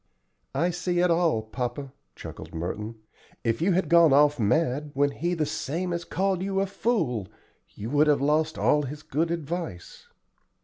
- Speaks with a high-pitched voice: No, medium, 150 Hz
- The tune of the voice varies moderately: Yes, average, 4.6 semitones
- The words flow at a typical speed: Yes, average, 170 wpm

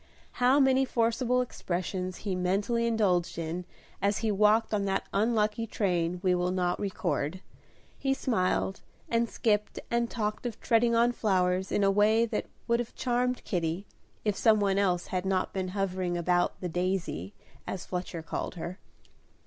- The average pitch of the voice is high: Yes, high, 195 Hz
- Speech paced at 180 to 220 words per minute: No, average, 160 wpm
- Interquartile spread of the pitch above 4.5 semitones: No, average, 4.1 semitones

